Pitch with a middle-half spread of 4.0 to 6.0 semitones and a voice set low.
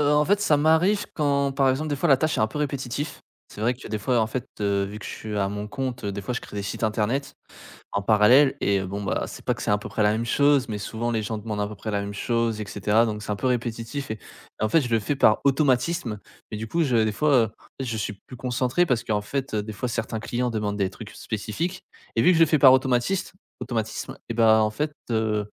Yes: average, 4.5 semitones; low, 115 Hz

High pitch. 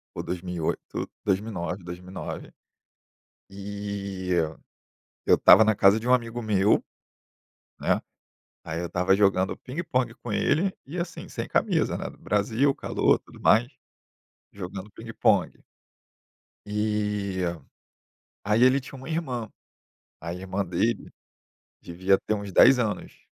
No: low, 105 Hz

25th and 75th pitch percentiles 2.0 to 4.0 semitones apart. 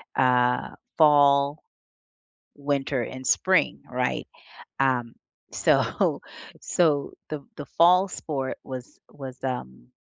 Yes: narrow, 2.6 semitones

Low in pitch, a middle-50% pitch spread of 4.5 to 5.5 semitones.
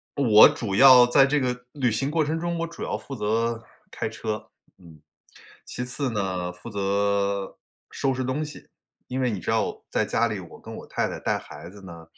Yes: low, 115 Hz; average, 5.1 semitones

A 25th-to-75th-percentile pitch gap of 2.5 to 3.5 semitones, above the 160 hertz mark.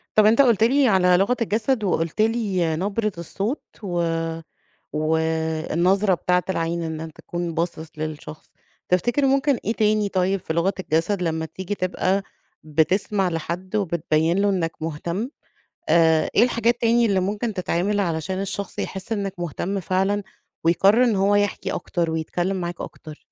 No: average, 3.9 semitones; medium, 185 Hz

